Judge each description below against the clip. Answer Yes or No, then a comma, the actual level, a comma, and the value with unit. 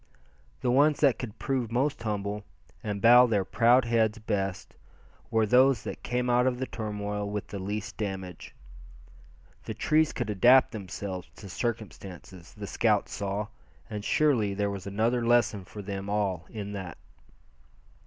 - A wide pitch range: No, average, 3.3 semitones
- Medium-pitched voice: No, low, 105 Hz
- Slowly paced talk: No, average, 155 wpm